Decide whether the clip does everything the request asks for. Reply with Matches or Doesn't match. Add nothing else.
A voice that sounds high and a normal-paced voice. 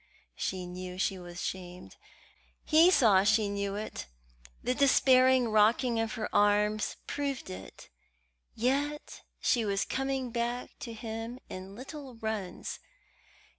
Doesn't match